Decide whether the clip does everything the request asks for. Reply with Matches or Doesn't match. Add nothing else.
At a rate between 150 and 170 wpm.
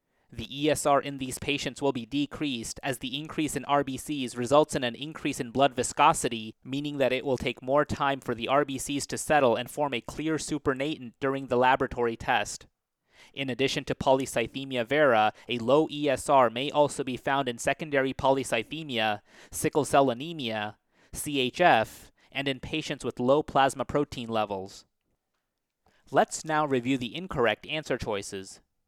Matches